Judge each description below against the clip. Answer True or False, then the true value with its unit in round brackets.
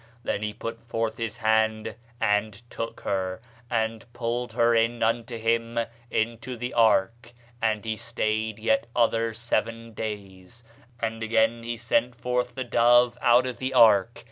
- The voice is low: True (115 Hz)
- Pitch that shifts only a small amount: True (1.3 semitones)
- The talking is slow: False (150 wpm)